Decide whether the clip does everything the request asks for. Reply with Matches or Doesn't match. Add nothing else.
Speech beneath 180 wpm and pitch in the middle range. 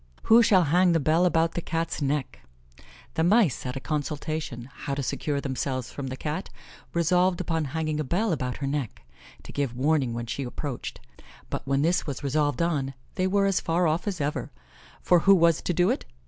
Doesn't match